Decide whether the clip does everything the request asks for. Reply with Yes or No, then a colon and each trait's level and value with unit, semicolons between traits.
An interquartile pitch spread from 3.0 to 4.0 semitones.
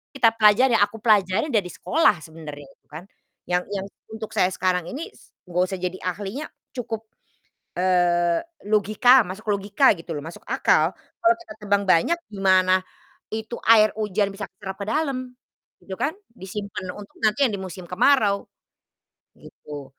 Yes: average, 3.5 semitones